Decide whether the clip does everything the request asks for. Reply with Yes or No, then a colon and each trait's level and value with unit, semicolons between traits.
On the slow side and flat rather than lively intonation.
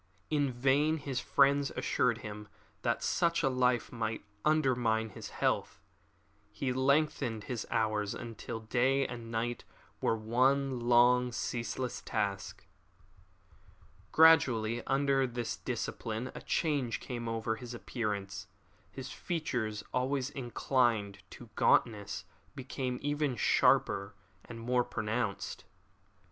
No: slow, 110 wpm; average, 3.2 semitones